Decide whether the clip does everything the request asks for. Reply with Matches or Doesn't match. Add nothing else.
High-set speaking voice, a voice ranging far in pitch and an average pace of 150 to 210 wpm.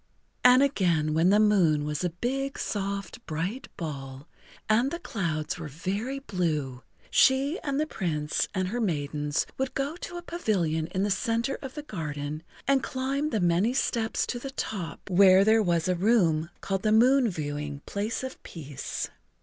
Matches